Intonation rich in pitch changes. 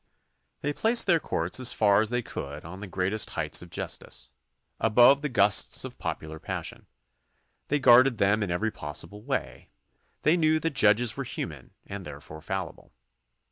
Yes: wide, 6.8 semitones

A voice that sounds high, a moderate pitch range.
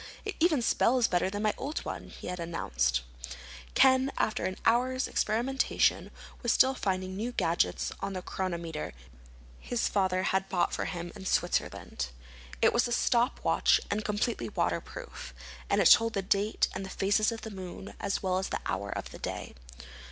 Yes: high, 200 Hz; average, 4.4 semitones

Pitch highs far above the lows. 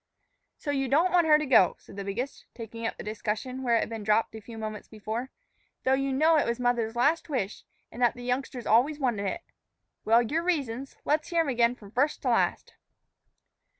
No: average, 4.1 semitones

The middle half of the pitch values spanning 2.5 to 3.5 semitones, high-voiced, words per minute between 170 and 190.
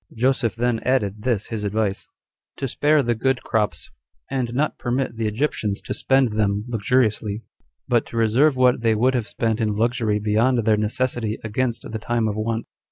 No: average, 2.9 semitones; low, 115 Hz; average, 175 wpm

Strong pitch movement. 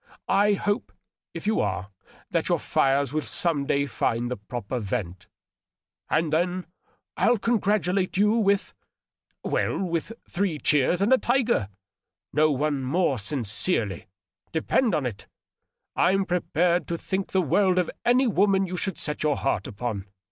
Yes: wide, 7.3 semitones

